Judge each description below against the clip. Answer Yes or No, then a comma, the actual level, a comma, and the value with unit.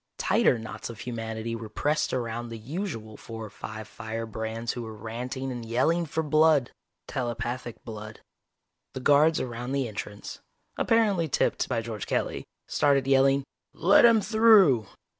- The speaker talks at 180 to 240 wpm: No, average, 145 wpm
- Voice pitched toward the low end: Yes, low, 120 Hz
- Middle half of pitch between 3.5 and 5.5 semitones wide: Yes, average, 4.6 semitones